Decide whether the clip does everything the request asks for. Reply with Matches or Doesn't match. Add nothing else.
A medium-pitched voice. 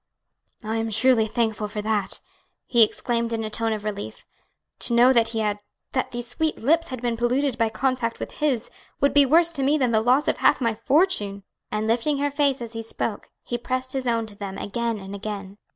Doesn't match